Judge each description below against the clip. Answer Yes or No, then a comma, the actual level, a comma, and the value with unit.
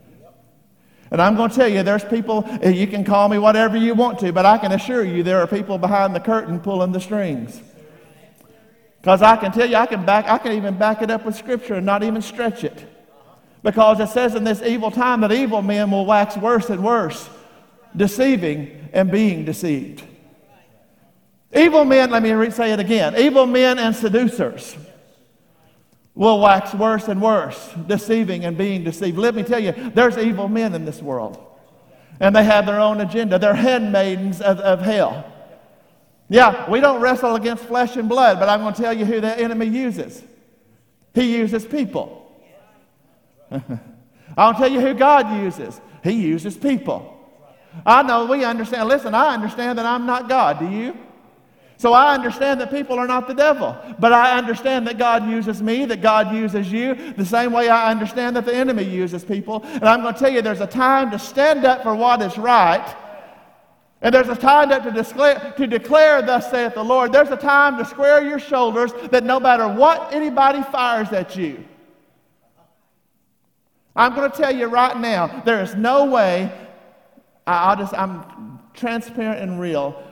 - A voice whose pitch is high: Yes, high, 225 Hz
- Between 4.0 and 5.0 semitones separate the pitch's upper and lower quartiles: No, average, 3.5 semitones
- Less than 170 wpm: No, average, 180 wpm